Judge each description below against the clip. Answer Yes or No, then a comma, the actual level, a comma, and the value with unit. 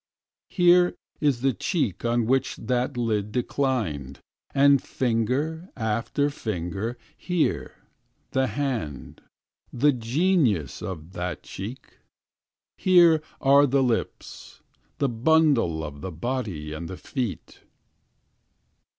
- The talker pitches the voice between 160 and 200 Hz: No, low, 120 Hz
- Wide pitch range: Yes, wide, 6.3 semitones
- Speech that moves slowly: Yes, slow, 105 wpm